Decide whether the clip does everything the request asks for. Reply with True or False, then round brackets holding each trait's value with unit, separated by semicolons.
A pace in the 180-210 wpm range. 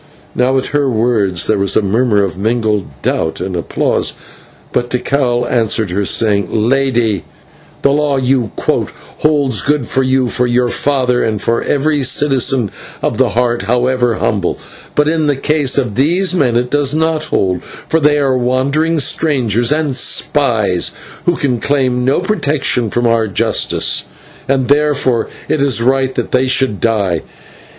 False (160 wpm)